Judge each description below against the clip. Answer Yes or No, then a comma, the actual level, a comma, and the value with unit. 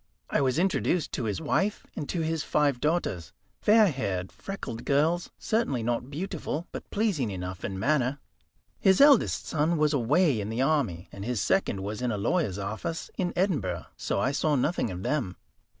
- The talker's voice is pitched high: No, medium, 140 Hz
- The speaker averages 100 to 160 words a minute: No, average, 180 wpm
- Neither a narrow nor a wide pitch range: No, wide, 7.9 semitones